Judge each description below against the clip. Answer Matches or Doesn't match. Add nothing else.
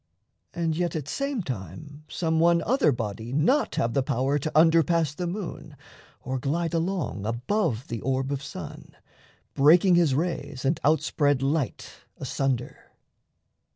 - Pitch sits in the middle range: Matches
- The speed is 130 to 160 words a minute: Matches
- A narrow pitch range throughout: Doesn't match